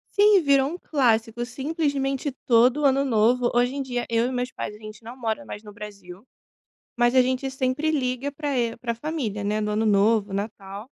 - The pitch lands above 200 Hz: Yes, high, 245 Hz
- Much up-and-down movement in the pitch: No, average, 4.0 semitones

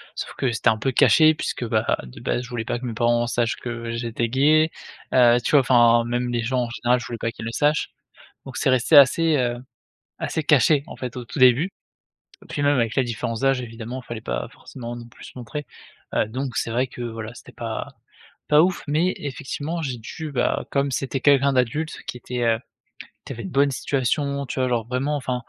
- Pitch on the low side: Yes, low, 125 Hz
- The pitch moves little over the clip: No, average, 3.1 semitones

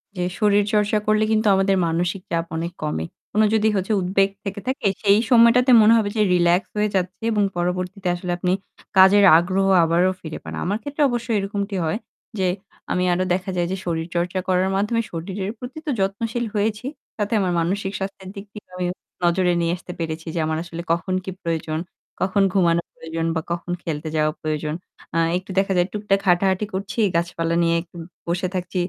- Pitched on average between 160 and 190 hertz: Yes, medium, 185 Hz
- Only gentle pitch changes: No, average, 3.0 semitones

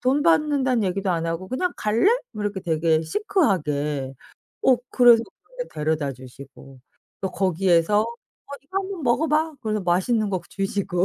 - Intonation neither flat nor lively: No, wide, 7.7 semitones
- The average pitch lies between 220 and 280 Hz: No, high, 195 Hz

